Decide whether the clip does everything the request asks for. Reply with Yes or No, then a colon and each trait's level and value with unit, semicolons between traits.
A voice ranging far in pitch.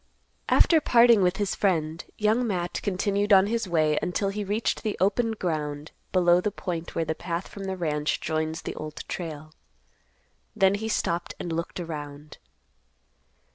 No: average, 4.3 semitones